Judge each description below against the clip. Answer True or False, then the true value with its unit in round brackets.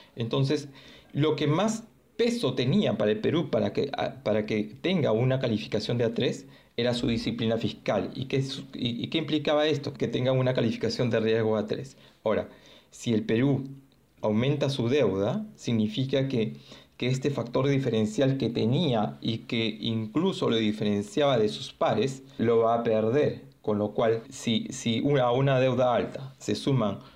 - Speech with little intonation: False (3.8 semitones)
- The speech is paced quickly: False (165 wpm)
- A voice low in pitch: True (125 Hz)